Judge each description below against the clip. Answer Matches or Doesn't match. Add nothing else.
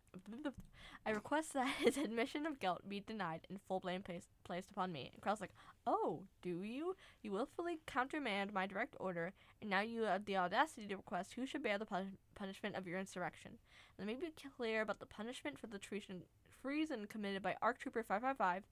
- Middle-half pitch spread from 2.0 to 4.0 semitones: Doesn't match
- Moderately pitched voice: Doesn't match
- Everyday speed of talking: Matches